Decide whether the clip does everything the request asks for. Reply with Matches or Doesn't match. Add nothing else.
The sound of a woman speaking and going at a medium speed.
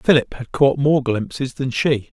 Doesn't match